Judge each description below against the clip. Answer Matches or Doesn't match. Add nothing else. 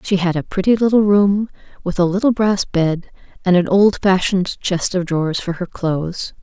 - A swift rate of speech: Doesn't match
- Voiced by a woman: Matches